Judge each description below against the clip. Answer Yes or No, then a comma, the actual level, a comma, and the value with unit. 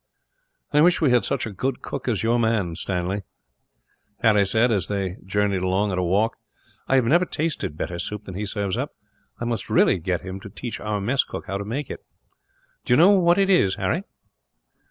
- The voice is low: Yes, low, 105 Hz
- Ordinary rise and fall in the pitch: Yes, average, 4.4 semitones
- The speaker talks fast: Yes, fast, 210 wpm